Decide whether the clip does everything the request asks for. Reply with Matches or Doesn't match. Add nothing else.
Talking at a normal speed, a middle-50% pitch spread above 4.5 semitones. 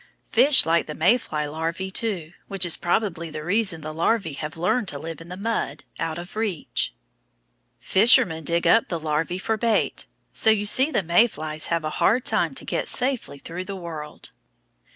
Matches